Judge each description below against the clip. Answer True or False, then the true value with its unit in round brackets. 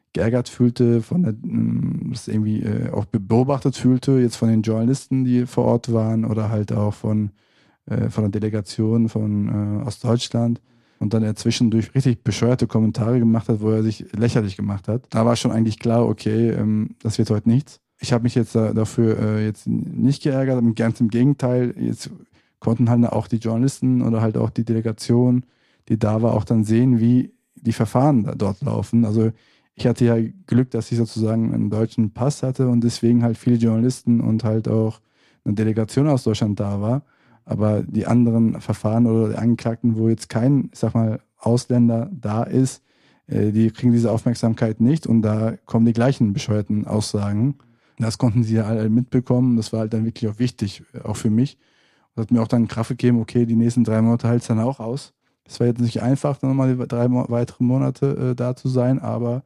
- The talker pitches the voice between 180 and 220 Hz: False (115 Hz)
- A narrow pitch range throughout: True (1.8 semitones)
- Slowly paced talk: False (190 wpm)